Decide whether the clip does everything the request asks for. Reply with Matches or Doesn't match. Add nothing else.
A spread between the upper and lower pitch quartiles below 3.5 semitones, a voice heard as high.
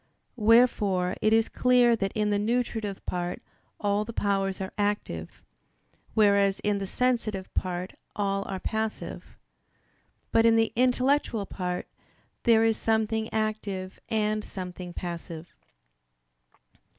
Matches